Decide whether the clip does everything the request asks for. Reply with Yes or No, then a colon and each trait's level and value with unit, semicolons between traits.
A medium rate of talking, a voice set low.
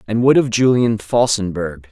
Yes: average, 155 wpm; low, 110 Hz